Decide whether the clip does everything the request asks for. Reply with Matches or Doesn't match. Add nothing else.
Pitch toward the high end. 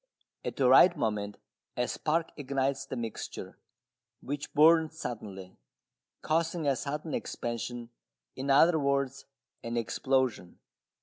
Doesn't match